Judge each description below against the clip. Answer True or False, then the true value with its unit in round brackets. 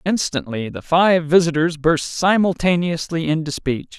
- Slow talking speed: True (120 wpm)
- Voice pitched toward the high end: False (165 Hz)